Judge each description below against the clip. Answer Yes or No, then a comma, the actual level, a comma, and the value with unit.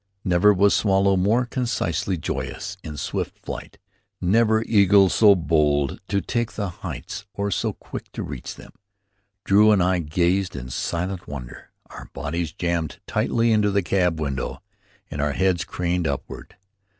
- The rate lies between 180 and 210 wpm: No, average, 150 wpm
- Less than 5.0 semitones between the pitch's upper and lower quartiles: Yes, average, 3.8 semitones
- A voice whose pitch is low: Yes, very low, 90 Hz